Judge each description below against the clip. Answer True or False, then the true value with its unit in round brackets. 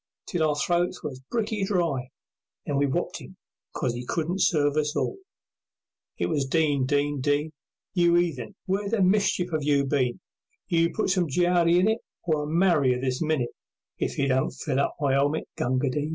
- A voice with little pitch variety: False (4.1 semitones)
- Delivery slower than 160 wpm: False (185 wpm)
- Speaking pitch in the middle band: True (155 Hz)